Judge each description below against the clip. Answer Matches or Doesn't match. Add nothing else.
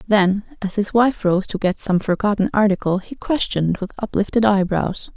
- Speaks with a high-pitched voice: Matches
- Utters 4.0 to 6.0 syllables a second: Matches